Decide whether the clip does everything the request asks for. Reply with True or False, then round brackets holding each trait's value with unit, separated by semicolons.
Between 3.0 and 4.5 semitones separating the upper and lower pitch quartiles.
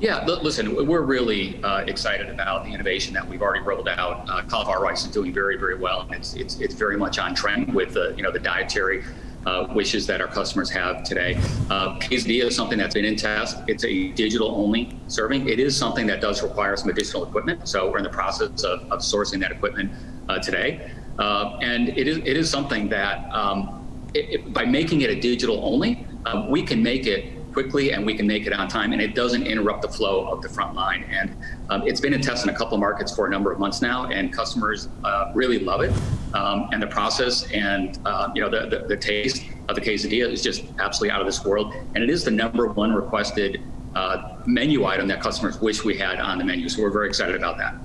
True (3.6 semitones)